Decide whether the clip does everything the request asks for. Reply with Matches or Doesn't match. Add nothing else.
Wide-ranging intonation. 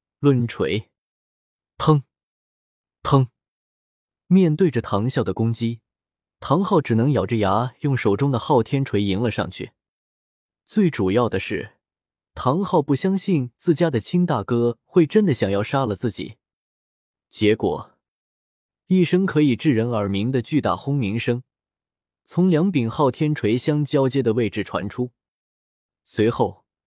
Matches